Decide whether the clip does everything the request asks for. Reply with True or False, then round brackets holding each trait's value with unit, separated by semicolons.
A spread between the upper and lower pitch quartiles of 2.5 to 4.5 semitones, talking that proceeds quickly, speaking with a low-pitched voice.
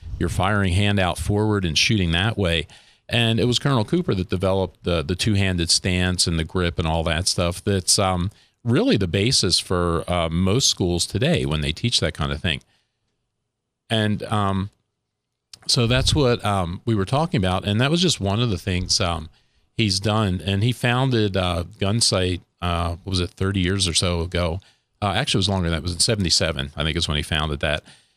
True (4.0 semitones; 210 wpm; 95 Hz)